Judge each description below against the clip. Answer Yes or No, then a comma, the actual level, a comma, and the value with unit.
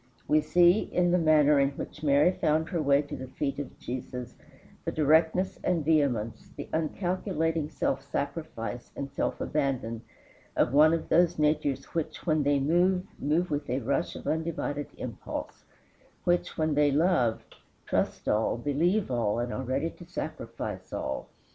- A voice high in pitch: No, medium, 150 Hz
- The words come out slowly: No, average, 160 wpm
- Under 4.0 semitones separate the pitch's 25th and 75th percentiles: Yes, average, 3.2 semitones